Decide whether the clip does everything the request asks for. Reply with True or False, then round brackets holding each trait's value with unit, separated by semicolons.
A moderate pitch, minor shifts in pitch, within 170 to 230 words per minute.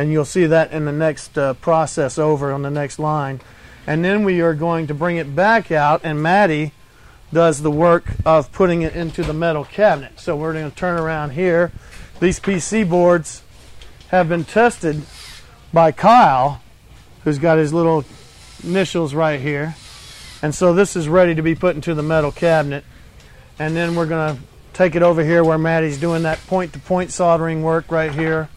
True (160 Hz; 2.3 semitones; 190 wpm)